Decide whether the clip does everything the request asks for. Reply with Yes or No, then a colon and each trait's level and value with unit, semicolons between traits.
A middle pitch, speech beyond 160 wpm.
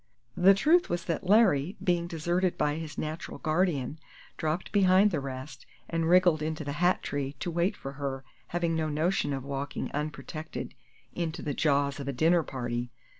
Yes: medium, 160 Hz; average, 175 wpm